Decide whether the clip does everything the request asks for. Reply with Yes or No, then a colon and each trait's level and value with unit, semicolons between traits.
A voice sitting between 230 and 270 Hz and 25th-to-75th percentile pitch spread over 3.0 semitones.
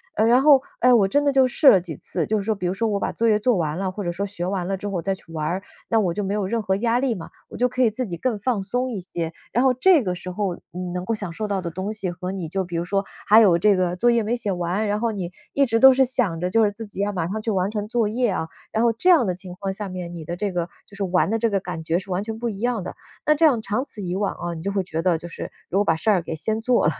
No: high, 200 Hz; average, 4.0 semitones